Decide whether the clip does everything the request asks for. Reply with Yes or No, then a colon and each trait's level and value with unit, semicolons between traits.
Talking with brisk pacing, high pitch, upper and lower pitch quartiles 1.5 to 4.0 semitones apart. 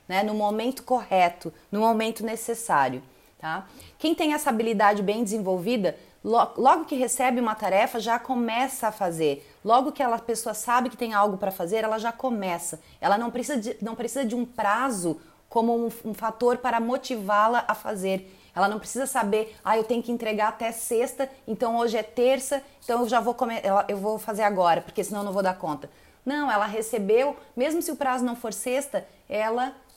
Yes: fast, 195 wpm; high, 230 Hz; average, 3.1 semitones